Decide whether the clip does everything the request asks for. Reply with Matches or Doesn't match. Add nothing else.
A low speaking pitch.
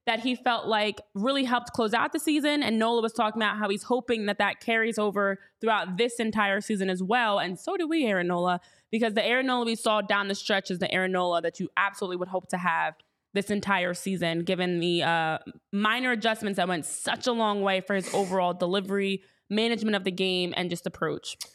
Doesn't match